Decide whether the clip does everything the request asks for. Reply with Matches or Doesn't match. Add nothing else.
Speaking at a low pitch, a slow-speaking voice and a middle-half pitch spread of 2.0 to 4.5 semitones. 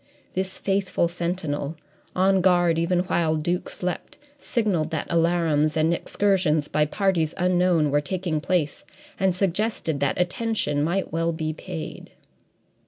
Doesn't match